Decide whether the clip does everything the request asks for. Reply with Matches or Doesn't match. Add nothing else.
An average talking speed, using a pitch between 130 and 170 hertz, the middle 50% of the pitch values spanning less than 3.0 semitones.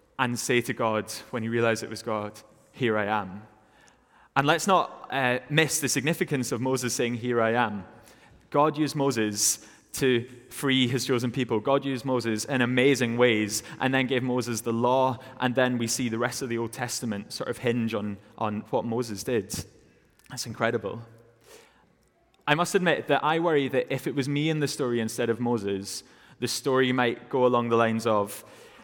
Doesn't match